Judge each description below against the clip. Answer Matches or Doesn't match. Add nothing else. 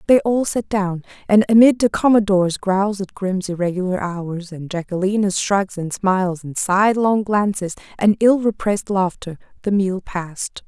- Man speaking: Doesn't match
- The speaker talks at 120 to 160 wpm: Matches